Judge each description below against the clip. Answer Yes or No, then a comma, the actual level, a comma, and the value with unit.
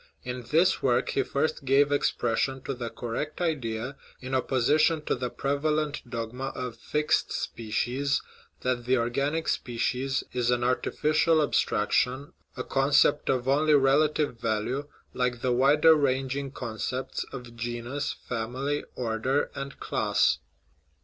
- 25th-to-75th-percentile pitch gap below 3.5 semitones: Yes, average, 2.9 semitones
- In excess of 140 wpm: No, slow, 135 wpm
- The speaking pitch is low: Yes, low, 130 Hz